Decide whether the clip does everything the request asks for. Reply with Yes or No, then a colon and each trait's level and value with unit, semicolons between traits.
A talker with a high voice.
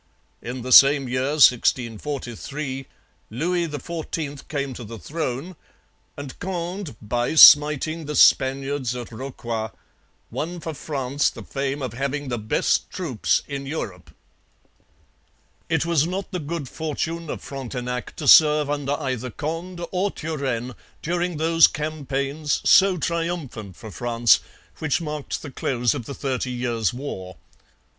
No: medium, 140 Hz